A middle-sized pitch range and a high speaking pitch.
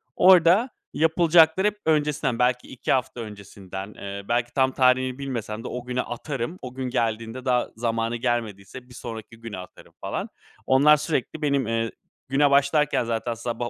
No: average, 3.5 semitones; low, 125 Hz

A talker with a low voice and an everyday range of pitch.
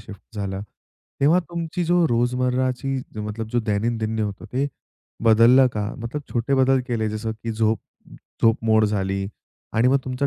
Yes: low, 115 Hz; average, 3.1 semitones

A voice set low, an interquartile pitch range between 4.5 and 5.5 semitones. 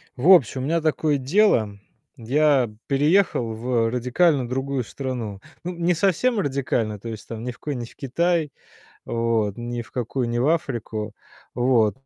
Yes: low, 130 Hz; average, 4.8 semitones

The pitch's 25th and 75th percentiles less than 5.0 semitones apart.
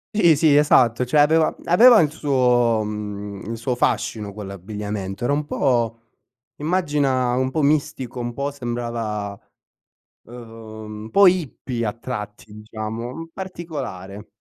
No: wide, 5.4 semitones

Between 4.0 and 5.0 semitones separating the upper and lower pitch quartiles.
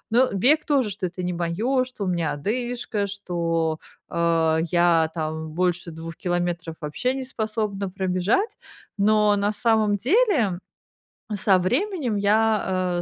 Yes: average, 4.5 semitones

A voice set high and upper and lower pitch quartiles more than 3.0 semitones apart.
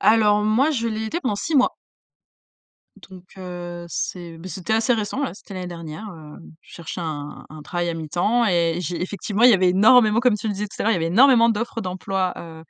Yes: high, 195 Hz; average, 4.2 semitones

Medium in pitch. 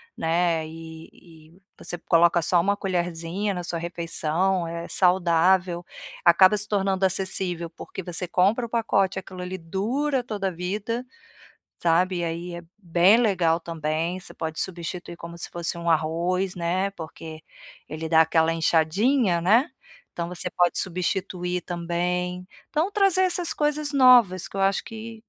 Yes: medium, 180 Hz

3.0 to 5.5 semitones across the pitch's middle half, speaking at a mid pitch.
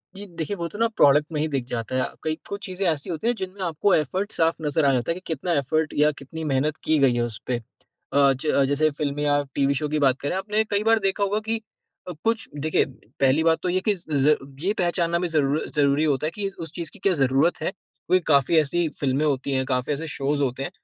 Yes: average, 4.4 semitones; medium, 155 Hz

